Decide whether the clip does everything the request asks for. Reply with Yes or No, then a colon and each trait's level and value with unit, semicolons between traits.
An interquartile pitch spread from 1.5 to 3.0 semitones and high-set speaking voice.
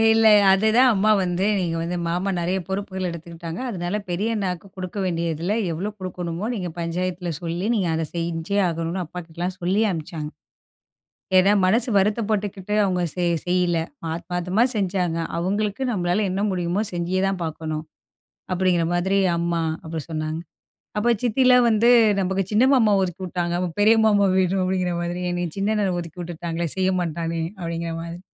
No: narrow, 2.6 semitones; medium, 180 Hz